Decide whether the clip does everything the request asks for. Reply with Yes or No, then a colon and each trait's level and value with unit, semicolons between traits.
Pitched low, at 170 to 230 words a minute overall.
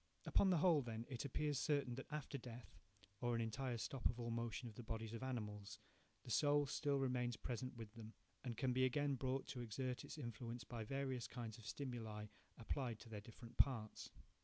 Yes: low, 120 Hz; average, 200 wpm